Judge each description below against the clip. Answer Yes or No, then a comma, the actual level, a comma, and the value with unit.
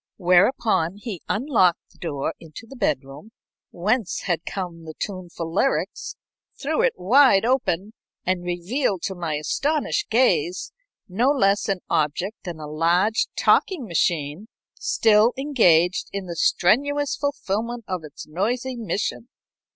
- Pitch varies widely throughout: Yes, wide, 5.8 semitones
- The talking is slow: Yes, slow, 130 wpm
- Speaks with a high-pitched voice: Yes, high, 195 Hz